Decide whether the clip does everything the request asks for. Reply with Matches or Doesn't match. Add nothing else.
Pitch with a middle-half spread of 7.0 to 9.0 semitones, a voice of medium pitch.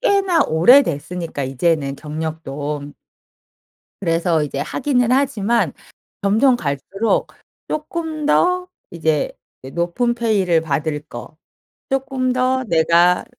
Matches